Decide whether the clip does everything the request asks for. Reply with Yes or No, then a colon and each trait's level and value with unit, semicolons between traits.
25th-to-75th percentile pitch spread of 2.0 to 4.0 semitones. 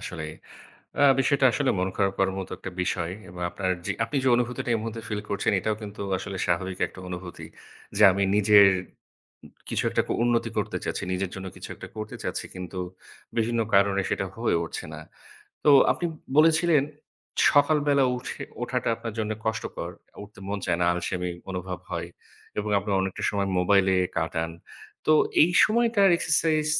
No: average, 4.8 semitones